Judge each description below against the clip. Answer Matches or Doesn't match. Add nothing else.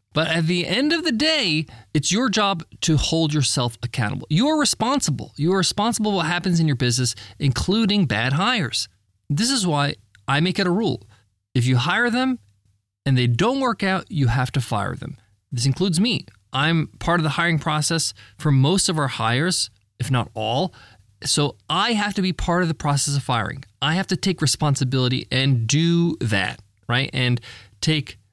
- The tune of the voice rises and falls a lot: Matches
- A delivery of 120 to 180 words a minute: Doesn't match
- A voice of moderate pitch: Matches